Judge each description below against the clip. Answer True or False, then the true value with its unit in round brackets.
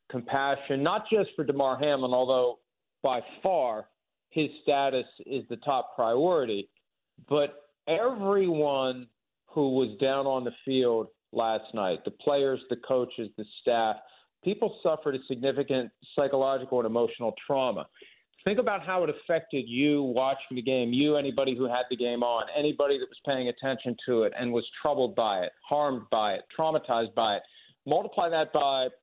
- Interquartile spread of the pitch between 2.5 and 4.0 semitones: True (2.8 semitones)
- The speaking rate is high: False (155 wpm)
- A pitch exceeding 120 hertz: True (135 Hz)